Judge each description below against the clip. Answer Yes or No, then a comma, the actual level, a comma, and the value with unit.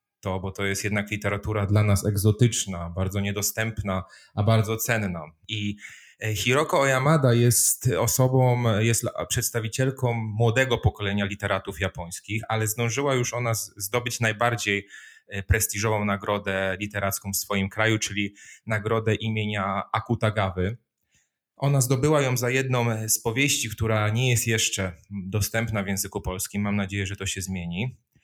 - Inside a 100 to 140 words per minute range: Yes, average, 130 wpm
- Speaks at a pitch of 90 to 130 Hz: Yes, low, 105 Hz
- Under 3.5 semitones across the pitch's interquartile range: Yes, average, 2.7 semitones